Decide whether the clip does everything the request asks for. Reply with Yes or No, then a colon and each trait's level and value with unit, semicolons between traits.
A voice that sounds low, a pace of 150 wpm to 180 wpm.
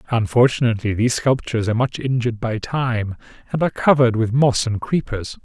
Yes: low, 120 Hz; average, 165 wpm